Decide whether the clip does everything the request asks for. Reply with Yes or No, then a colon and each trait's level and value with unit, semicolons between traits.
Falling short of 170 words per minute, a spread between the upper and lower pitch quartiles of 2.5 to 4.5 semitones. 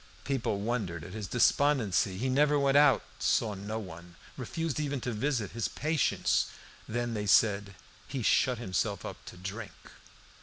No: average, 155 wpm; wide, 5.5 semitones